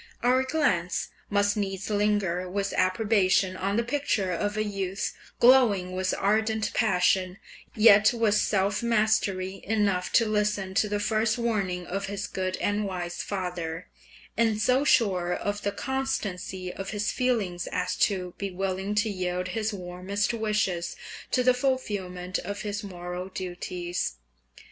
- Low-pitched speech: No, high, 200 Hz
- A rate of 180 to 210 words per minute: No, average, 145 wpm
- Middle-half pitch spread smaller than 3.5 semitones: Yes, average, 2.7 semitones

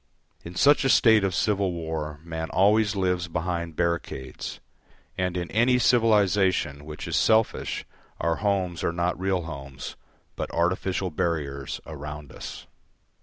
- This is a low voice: Yes, very low, 90 Hz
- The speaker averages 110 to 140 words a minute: Yes, slow, 135 wpm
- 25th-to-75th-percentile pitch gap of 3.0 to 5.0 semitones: Yes, average, 3.4 semitones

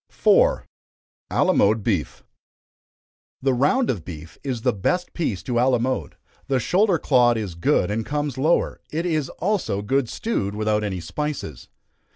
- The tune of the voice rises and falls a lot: Yes, wide, 6.9 semitones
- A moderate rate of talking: Yes, average, 145 wpm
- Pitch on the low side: Yes, low, 125 Hz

